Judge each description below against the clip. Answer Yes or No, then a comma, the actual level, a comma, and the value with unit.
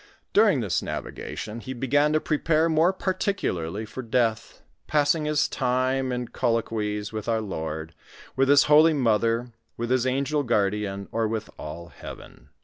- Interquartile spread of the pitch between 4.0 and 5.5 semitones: Yes, average, 5.2 semitones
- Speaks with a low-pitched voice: Yes, low, 125 Hz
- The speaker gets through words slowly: No, average, 150 wpm